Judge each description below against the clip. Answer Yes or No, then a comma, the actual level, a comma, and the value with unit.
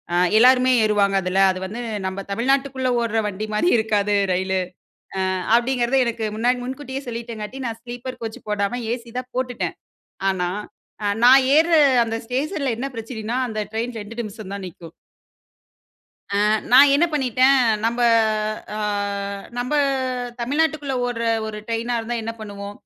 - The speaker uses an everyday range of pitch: Yes, average, 3.3 semitones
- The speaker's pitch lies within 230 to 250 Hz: Yes, high, 235 Hz